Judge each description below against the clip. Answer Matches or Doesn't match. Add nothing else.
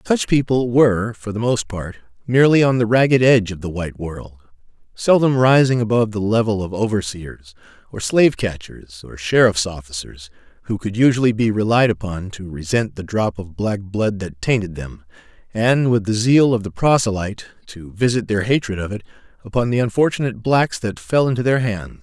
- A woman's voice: Doesn't match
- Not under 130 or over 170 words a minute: Doesn't match